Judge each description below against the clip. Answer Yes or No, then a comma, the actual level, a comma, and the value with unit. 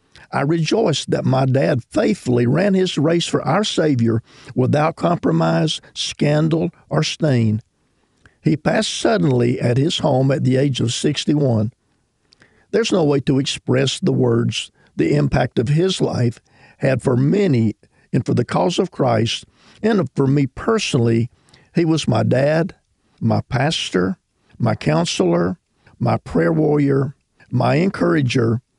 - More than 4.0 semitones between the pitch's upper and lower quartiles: Yes, average, 4.8 semitones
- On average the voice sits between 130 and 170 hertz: Yes, low, 135 Hz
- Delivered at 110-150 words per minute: Yes, average, 140 wpm